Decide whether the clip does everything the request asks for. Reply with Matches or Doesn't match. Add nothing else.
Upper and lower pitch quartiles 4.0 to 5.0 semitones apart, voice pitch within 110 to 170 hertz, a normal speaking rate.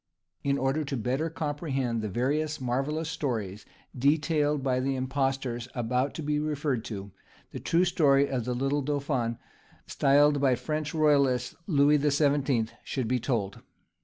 Doesn't match